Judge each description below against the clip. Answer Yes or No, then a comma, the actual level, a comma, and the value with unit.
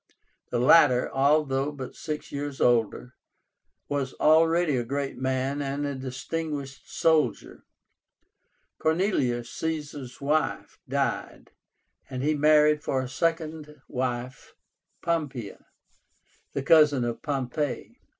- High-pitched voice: No, medium, 140 Hz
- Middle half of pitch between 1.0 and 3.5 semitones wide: Yes, average, 2.9 semitones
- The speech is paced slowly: Yes, slow, 105 wpm